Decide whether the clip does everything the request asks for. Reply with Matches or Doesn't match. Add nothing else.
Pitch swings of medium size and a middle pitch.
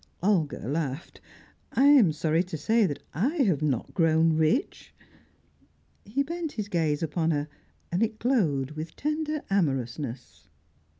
Doesn't match